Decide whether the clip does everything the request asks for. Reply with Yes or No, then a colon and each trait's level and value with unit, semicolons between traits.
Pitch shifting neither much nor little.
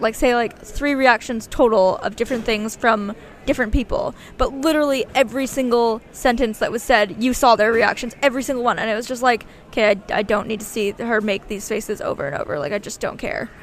Yes: average, 3.2 semitones